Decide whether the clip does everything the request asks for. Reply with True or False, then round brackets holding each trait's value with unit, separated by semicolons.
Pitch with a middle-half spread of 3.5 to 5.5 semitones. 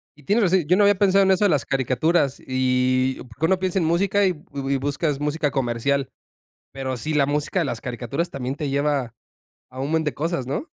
True (4.7 semitones)